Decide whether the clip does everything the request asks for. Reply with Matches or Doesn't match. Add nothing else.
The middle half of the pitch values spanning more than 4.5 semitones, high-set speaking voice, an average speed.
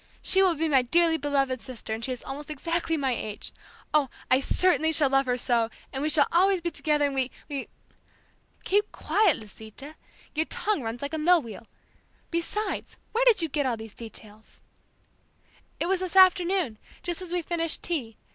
Matches